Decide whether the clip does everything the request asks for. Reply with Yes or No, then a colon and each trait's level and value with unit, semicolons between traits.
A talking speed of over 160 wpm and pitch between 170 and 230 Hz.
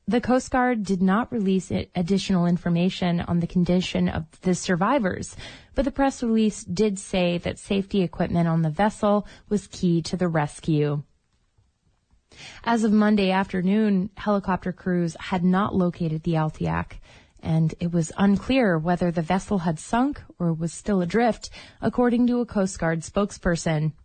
No: average, 150 wpm; medium, 185 Hz